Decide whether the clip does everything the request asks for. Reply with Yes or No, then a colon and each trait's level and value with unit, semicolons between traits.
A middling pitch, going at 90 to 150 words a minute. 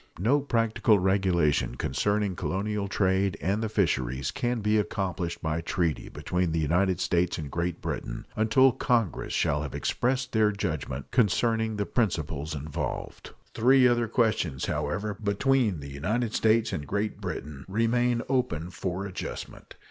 No: low, 100 Hz; average, 140 wpm